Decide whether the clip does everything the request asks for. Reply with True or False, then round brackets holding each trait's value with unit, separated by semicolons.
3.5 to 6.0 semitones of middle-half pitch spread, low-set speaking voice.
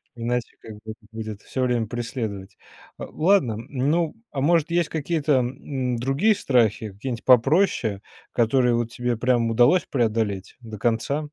True (3.8 semitones; 125 Hz)